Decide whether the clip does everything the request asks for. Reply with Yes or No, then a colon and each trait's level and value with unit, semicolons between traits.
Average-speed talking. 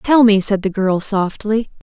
Yes: average, 190 wpm